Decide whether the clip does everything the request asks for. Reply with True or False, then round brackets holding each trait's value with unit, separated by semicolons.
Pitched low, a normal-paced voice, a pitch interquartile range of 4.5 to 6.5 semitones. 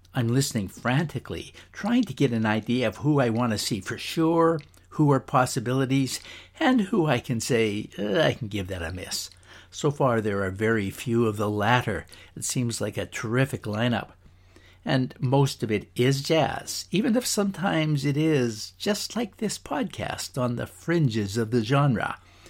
True (120 Hz; 180 wpm; 5.6 semitones)